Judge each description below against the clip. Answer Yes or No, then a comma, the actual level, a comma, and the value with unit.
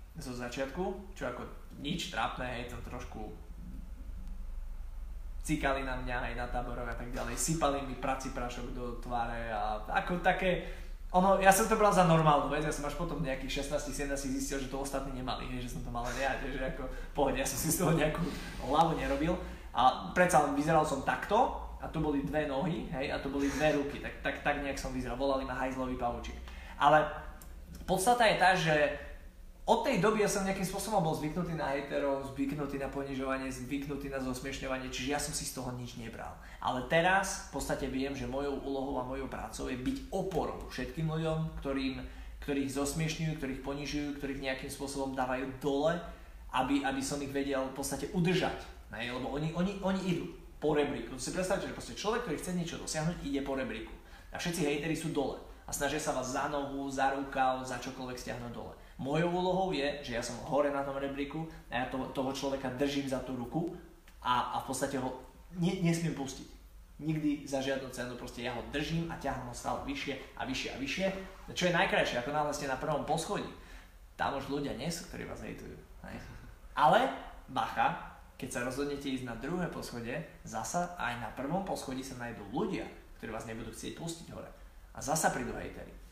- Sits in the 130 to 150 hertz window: Yes, medium, 140 Hz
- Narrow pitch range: No, average, 3.4 semitones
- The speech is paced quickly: Yes, fast, 195 wpm